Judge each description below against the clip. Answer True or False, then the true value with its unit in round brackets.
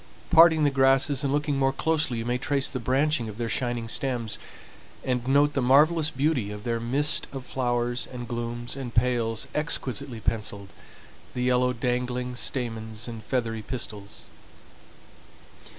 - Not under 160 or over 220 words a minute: False (150 wpm)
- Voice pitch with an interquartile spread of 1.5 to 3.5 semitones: True (2.8 semitones)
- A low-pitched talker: True (125 Hz)